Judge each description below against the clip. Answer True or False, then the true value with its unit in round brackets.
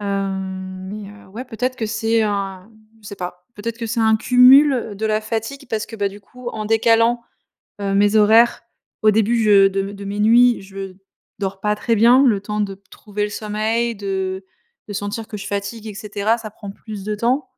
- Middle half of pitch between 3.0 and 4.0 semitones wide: False (2.4 semitones)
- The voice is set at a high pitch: True (210 Hz)